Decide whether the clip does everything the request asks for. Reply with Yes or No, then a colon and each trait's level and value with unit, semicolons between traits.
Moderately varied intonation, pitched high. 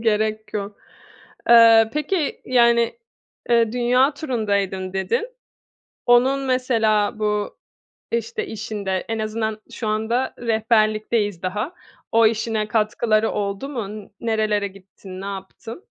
No: narrow, 2.1 semitones; high, 220 Hz